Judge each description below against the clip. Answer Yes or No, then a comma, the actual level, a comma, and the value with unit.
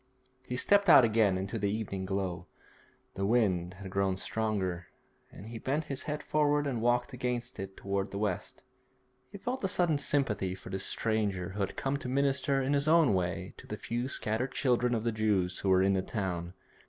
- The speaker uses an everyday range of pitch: No, wide, 5.7 semitones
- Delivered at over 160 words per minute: Yes, average, 200 wpm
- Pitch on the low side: Yes, low, 110 Hz